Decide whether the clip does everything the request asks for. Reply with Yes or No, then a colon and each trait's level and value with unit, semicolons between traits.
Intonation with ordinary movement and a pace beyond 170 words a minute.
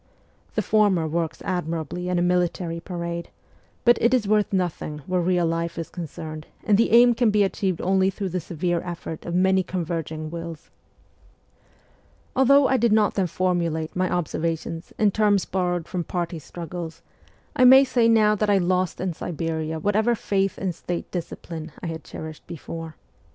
No: average, 3.2 semitones; average, 165 wpm